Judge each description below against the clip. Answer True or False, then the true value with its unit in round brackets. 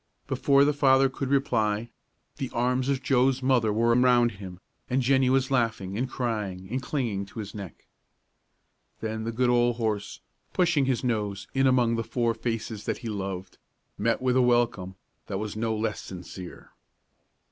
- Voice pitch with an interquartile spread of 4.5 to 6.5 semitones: False (3.4 semitones)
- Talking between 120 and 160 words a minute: False (170 wpm)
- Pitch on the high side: False (120 Hz)